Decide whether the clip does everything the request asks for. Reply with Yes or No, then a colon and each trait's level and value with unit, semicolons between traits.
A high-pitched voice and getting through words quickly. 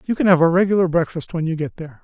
No: medium, 165 Hz; fast, 295 wpm